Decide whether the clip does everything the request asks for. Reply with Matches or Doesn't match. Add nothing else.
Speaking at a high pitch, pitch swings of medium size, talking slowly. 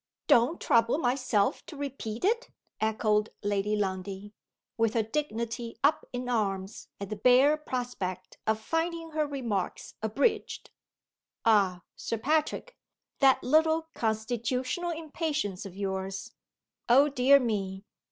Doesn't match